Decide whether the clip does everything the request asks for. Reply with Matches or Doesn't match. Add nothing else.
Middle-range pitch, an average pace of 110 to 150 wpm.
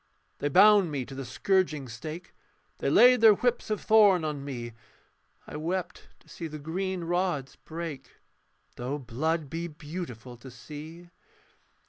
Matches